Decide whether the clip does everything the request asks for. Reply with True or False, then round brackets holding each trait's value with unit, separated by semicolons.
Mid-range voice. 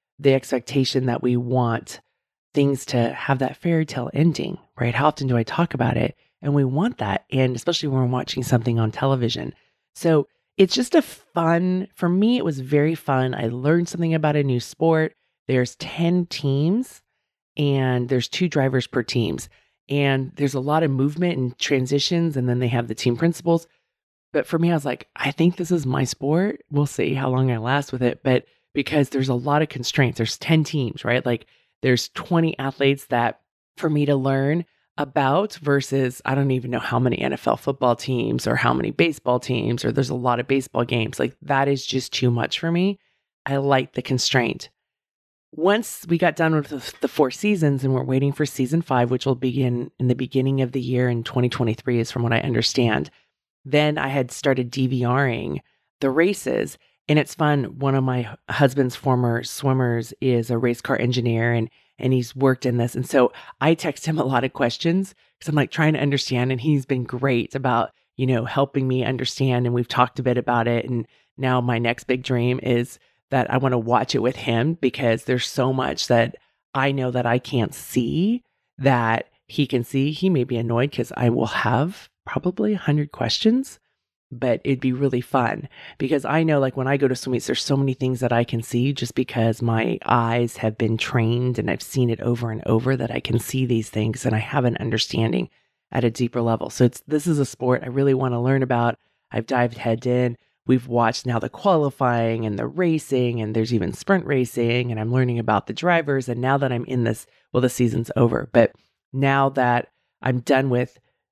False (130 Hz)